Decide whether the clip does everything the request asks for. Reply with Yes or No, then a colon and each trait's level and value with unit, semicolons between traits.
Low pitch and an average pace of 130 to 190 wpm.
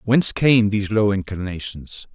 Yes: low, 105 Hz; average, 140 wpm